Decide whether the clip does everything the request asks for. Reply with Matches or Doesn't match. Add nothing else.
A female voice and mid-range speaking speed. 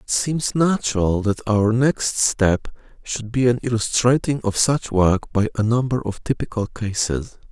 Doesn't match